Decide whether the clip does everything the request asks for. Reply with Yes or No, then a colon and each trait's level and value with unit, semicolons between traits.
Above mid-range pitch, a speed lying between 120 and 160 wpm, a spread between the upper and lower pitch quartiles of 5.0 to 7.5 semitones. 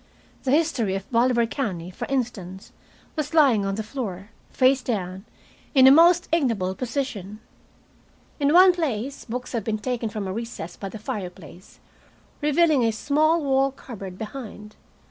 Yes: high, 235 Hz; average, 150 wpm; wide, 5.6 semitones